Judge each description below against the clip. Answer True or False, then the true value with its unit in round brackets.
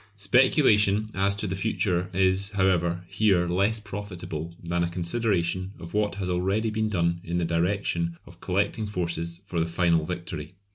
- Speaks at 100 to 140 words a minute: False (160 wpm)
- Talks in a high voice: False (95 Hz)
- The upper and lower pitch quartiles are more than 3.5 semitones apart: False (3.1 semitones)